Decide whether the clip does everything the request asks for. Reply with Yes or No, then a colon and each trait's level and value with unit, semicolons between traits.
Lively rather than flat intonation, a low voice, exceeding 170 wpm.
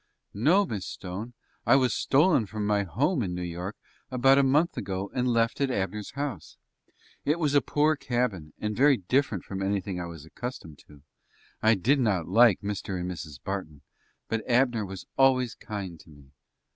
Yes: wide, 6.0 semitones; low, 105 Hz; average, 180 wpm